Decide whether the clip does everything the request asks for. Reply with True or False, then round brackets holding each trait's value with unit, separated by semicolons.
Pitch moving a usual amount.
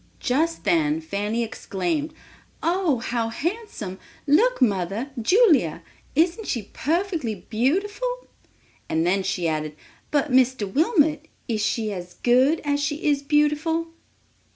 False (7.2 semitones)